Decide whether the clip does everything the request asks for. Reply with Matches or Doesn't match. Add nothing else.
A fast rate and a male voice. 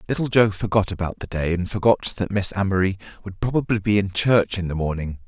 Matches